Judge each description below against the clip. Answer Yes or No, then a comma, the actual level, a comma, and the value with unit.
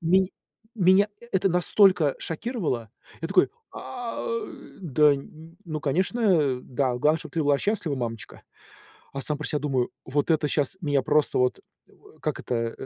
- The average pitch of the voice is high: No, medium, 150 Hz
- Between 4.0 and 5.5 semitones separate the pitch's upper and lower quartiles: Yes, average, 5.2 semitones